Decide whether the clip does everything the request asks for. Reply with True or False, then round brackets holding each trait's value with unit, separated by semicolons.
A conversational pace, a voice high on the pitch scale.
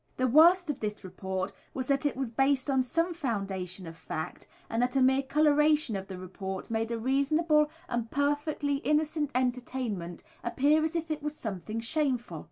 True (175 wpm; 260 Hz)